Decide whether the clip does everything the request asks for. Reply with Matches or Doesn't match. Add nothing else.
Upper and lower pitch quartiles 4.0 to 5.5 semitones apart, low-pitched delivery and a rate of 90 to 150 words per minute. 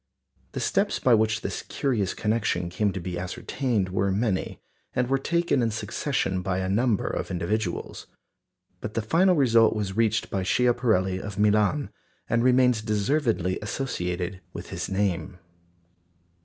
Matches